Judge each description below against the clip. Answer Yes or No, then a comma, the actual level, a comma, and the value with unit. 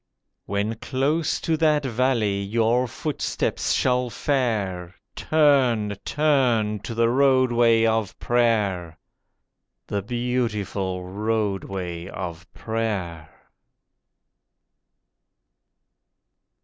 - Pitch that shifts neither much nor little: Yes, average, 4.2 semitones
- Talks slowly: Yes, slow, 75 wpm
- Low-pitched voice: Yes, low, 115 Hz